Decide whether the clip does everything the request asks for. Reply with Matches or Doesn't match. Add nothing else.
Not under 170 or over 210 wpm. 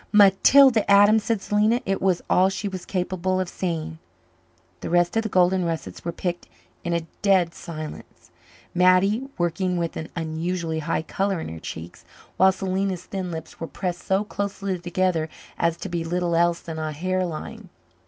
Matches